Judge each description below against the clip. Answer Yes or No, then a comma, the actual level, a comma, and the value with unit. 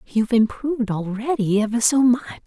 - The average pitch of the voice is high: Yes, high, 235 Hz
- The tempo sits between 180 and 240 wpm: No, average, 145 wpm